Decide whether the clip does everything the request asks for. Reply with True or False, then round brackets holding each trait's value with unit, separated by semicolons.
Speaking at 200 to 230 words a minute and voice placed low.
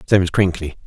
True (210 wpm; 90 Hz)